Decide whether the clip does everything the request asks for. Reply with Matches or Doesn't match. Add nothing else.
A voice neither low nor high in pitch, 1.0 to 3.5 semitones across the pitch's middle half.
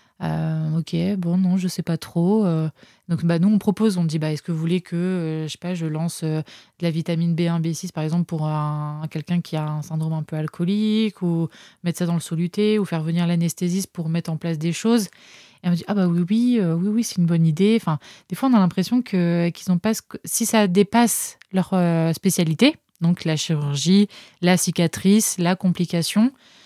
Matches